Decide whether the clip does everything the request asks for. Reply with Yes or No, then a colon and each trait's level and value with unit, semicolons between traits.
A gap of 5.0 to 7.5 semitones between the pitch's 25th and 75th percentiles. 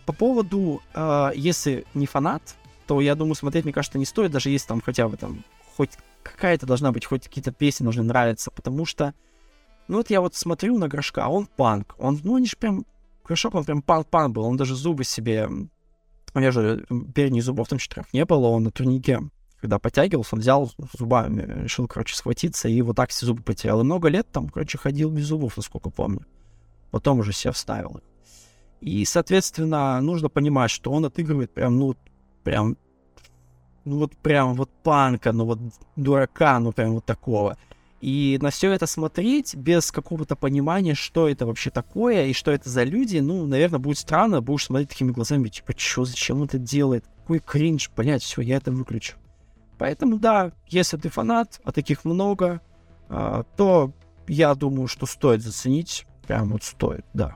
Yes: wide, 5.4 semitones